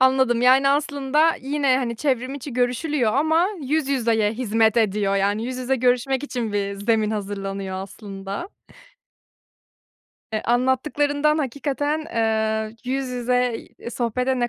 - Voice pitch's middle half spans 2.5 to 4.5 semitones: Yes, average, 3.8 semitones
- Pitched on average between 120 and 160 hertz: No, very high, 250 Hz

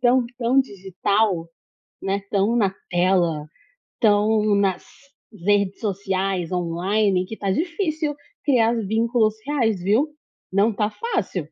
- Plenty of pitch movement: No, average, 3.4 semitones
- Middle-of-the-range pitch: No, high, 205 Hz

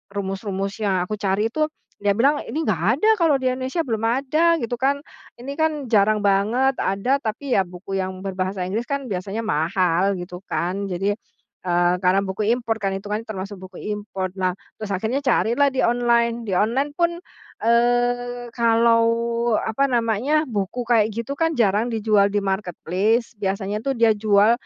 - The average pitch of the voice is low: No, high, 220 Hz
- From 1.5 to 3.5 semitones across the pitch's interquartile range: No, average, 4.0 semitones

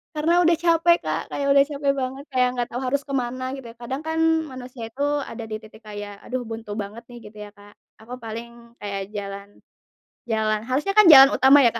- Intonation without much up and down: No, average, 4.2 semitones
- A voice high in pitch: Yes, very high, 250 Hz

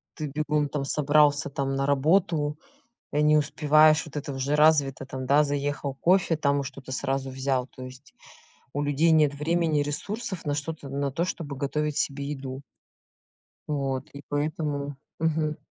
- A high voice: No, medium, 145 Hz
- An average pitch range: No, narrow, 1.8 semitones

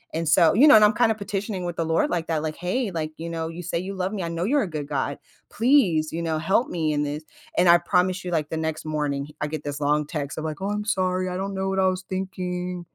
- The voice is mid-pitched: Yes, medium, 175 Hz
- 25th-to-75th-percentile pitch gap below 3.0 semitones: No, average, 3.5 semitones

